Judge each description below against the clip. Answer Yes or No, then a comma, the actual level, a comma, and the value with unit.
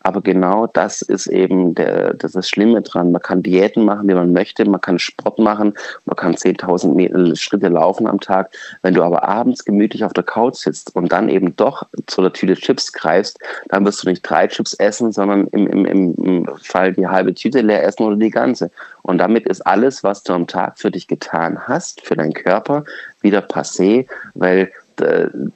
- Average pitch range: No, narrow, 2.3 semitones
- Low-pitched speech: Yes, very low, 95 Hz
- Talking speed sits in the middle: No, fast, 200 wpm